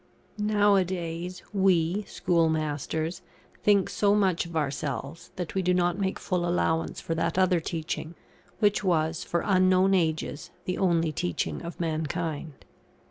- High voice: No, medium, 175 Hz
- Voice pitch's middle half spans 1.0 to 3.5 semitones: Yes, average, 2.7 semitones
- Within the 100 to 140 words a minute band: Yes, slow, 135 wpm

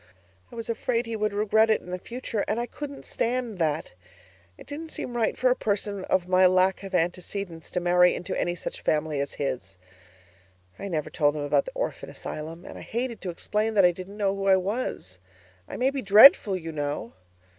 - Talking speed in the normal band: No, fast, 210 wpm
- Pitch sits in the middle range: No, high, 195 Hz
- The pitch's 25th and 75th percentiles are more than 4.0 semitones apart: Yes, average, 4.7 semitones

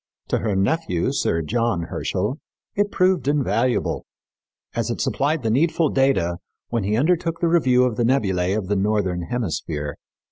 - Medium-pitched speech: No, low, 115 Hz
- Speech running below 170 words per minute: Yes, average, 155 wpm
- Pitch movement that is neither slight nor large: No, wide, 6.8 semitones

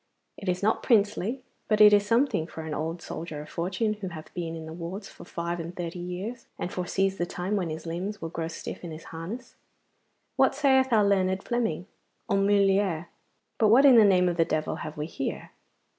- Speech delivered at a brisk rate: Yes, fast, 215 wpm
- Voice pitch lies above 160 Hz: Yes, medium, 185 Hz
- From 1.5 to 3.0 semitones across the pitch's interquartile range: No, average, 3.8 semitones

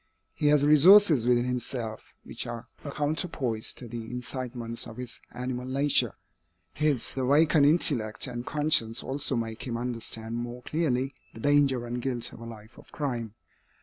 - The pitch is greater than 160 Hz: No, low, 125 Hz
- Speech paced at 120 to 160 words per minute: Yes, average, 155 wpm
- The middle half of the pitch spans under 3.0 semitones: No, average, 3.7 semitones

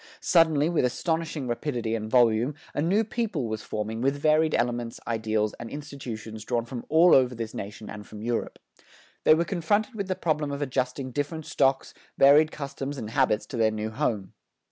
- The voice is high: No, low, 130 Hz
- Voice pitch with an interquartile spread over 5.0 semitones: Yes, wide, 5.4 semitones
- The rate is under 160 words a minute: No, average, 180 wpm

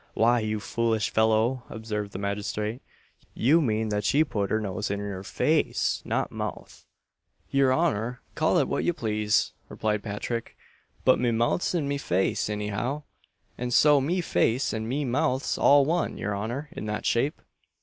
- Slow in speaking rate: No, average, 170 wpm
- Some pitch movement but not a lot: Yes, average, 4.4 semitones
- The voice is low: Yes, low, 115 Hz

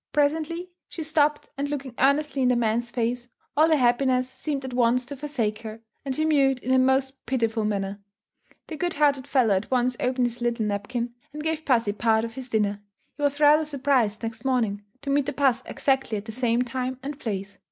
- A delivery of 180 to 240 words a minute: Yes, fast, 205 wpm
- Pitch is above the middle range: Yes, very high, 255 Hz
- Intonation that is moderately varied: Yes, average, 3.7 semitones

